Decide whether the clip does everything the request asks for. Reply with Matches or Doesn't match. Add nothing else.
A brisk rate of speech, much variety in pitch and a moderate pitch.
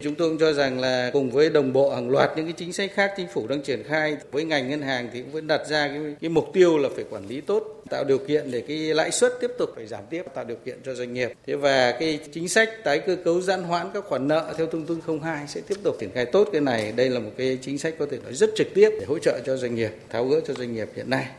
Matches